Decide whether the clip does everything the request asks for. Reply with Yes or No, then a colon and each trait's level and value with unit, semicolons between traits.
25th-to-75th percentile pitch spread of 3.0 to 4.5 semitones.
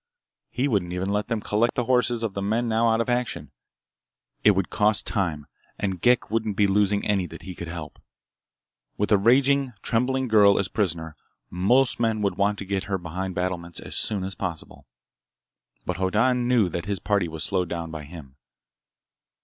Yes: average, 4.1 semitones